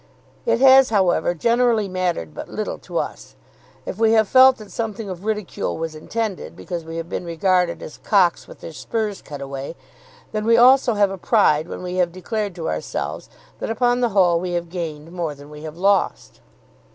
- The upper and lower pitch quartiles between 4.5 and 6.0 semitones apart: Yes, average, 5.0 semitones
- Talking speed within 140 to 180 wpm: No, average, 195 wpm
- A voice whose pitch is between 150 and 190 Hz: Yes, medium, 185 Hz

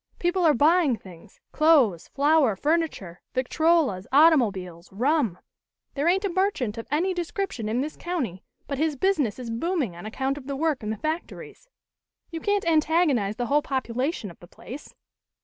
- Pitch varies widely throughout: Yes, wide, 6.5 semitones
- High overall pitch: Yes, very high, 280 Hz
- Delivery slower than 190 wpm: Yes, average, 165 wpm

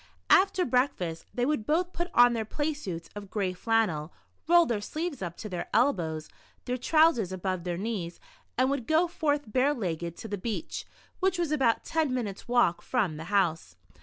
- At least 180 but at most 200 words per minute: Yes, average, 185 wpm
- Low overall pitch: No, high, 230 Hz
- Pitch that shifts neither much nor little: No, wide, 8.4 semitones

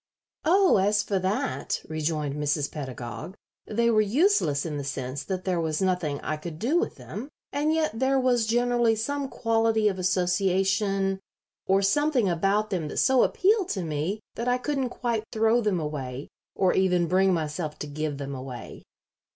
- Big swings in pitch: Yes, wide, 7.1 semitones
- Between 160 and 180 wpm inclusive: Yes, average, 170 wpm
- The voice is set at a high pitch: Yes, high, 195 Hz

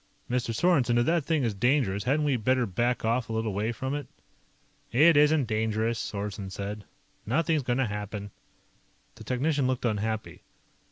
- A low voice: Yes, low, 120 Hz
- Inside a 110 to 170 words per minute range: Yes, average, 165 wpm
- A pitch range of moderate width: Yes, average, 4.2 semitones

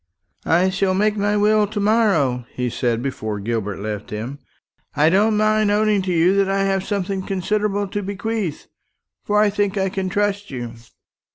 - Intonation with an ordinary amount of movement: No, wide, 6.2 semitones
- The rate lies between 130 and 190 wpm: Yes, average, 175 wpm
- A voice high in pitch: Yes, high, 195 Hz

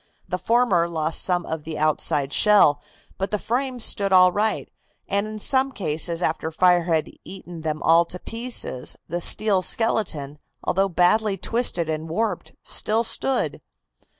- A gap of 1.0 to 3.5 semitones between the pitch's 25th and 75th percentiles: No, average, 5.1 semitones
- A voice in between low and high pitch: Yes, medium, 180 Hz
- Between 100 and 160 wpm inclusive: Yes, average, 150 wpm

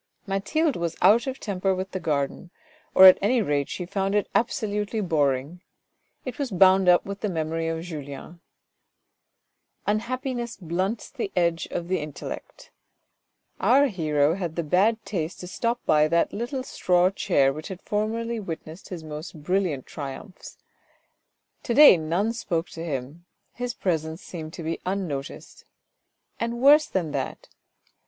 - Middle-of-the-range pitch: Yes, medium, 180 Hz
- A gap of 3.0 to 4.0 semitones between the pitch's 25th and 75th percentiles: No, average, 4.9 semitones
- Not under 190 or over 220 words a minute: No, average, 150 wpm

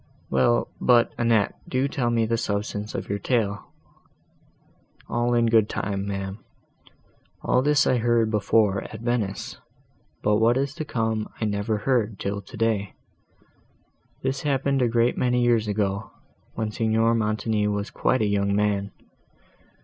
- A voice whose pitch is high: No, low, 110 Hz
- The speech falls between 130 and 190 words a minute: Yes, average, 145 wpm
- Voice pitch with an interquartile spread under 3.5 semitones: Yes, average, 2.7 semitones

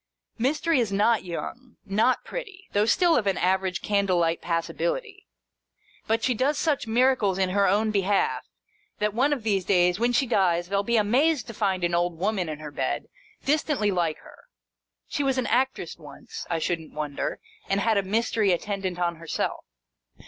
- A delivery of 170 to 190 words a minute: Yes, average, 180 wpm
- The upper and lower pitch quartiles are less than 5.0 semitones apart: No, wide, 5.6 semitones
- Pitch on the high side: Yes, high, 205 Hz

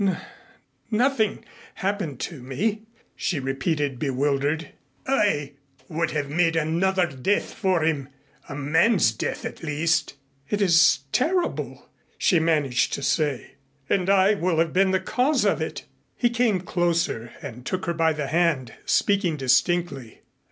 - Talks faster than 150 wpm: No, average, 140 wpm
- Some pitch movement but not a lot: Yes, average, 5.0 semitones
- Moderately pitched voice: Yes, medium, 165 Hz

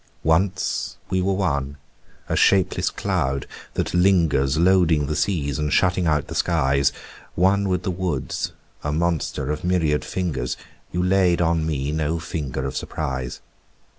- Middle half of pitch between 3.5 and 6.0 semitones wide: Yes, average, 4.1 semitones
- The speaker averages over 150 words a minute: No, average, 145 wpm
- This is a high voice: No, very low, 80 Hz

